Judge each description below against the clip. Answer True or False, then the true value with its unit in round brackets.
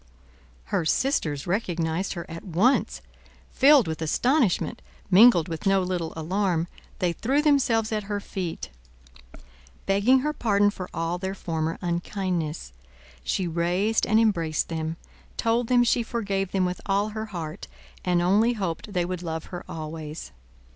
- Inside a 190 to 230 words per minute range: False (145 wpm)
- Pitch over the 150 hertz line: True (185 Hz)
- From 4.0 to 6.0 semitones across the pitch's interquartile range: True (4.6 semitones)